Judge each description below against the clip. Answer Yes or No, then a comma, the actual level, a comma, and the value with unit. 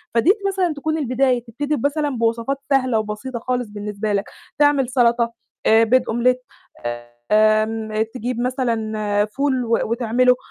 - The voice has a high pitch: Yes, high, 240 Hz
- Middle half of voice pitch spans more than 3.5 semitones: No, average, 3.2 semitones